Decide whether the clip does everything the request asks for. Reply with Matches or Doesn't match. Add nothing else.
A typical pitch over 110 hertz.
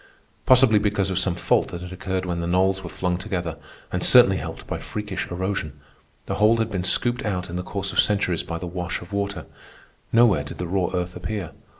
Doesn't match